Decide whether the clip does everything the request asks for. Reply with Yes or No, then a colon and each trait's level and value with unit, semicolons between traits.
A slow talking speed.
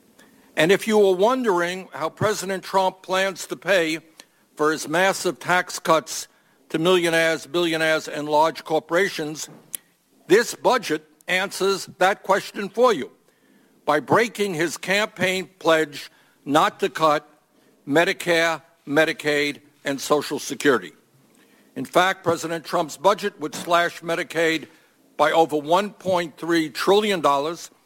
Yes: slow, 120 wpm